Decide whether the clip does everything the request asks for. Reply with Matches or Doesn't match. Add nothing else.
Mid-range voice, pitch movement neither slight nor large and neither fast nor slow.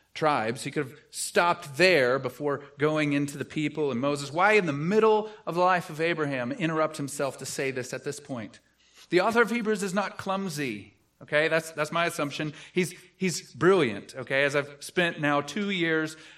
Matches